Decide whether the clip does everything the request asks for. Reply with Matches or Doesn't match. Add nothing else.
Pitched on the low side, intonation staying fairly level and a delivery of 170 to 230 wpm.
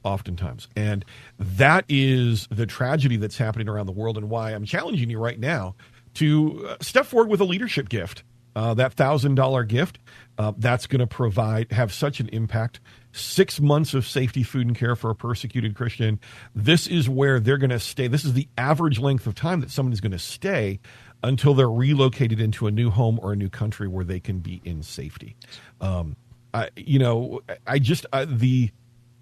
Doesn't match